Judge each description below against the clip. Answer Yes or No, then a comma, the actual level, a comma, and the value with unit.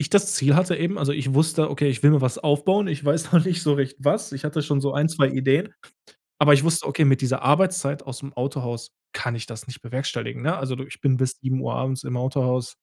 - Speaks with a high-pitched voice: No, medium, 140 Hz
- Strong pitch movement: No, average, 2.8 semitones